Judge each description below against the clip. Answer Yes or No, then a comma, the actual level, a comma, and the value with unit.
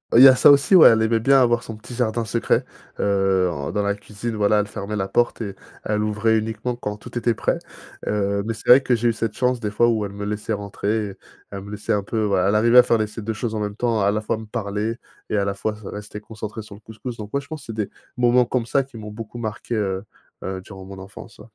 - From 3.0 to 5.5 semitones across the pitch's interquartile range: No, narrow, 2.4 semitones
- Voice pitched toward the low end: Yes, low, 110 Hz